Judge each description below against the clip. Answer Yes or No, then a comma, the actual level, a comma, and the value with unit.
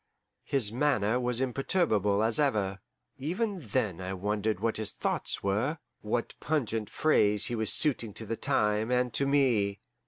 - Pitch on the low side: Yes, low, 115 Hz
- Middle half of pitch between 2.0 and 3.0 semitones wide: No, average, 4.4 semitones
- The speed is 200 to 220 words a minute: No, average, 155 wpm